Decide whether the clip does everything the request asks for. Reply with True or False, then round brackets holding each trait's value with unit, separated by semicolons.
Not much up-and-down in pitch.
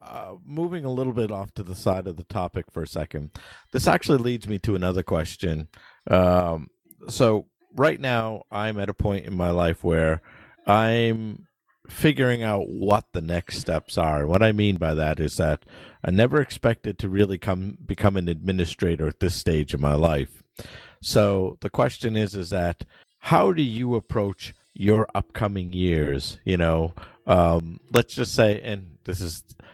False (4.3 semitones)